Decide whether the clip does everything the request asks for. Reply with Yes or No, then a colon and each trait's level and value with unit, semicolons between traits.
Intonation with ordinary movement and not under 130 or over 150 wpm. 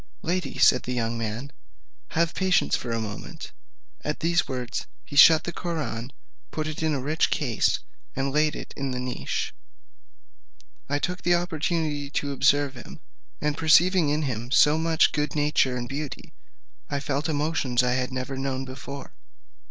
No: average, 3.5 semitones; average, 165 wpm